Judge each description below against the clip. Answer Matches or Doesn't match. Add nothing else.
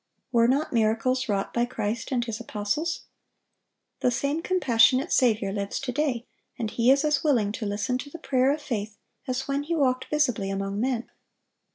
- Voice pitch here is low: Doesn't match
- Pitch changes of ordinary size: Matches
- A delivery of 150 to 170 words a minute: Doesn't match